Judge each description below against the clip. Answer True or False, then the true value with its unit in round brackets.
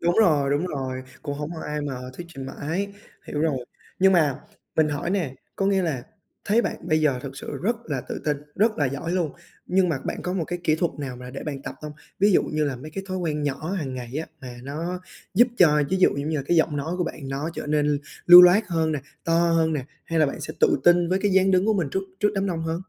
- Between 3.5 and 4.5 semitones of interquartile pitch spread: True (3.9 semitones)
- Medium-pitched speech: True (160 Hz)